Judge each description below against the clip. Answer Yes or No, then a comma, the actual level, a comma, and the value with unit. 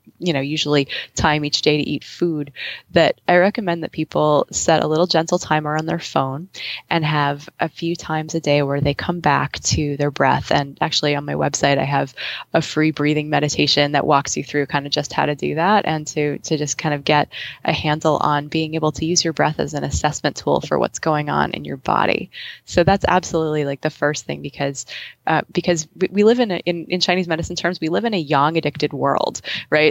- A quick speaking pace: Yes, fast, 225 wpm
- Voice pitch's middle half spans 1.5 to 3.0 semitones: Yes, average, 2.7 semitones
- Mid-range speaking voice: Yes, medium, 155 Hz